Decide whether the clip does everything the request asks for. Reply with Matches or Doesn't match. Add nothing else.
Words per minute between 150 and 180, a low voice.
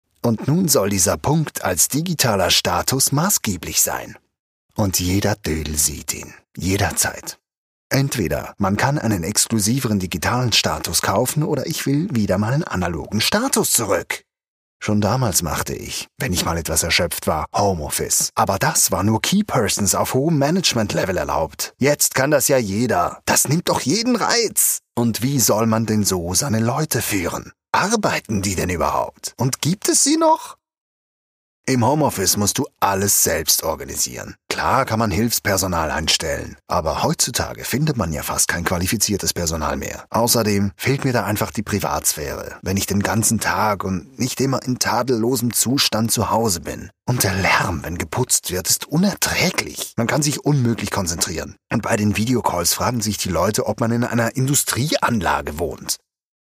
Matches